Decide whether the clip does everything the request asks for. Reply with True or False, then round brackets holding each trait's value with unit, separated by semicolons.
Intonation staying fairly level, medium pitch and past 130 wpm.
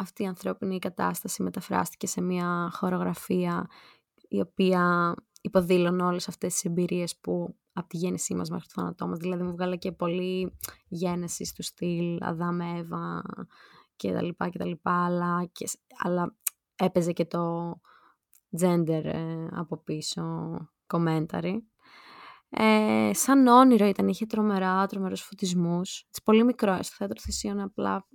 True (2.0 semitones; 180 Hz; 140 wpm)